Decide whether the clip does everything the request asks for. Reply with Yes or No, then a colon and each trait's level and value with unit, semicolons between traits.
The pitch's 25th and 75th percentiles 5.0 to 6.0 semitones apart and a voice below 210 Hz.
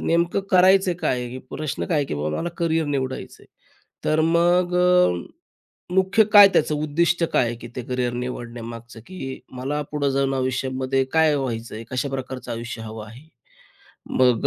Yes: average, 5.3 semitones; low, 135 Hz